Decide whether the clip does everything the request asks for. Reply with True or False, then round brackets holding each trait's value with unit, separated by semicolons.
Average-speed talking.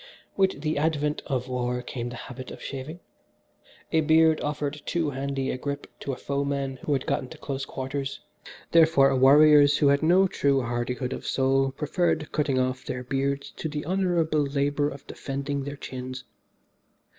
True (170 wpm)